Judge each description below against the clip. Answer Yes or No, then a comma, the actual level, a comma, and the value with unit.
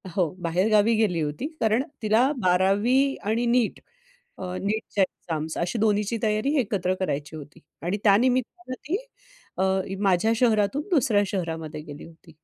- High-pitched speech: Yes, high, 205 Hz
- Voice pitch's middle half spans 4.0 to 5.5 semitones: Yes, average, 4.7 semitones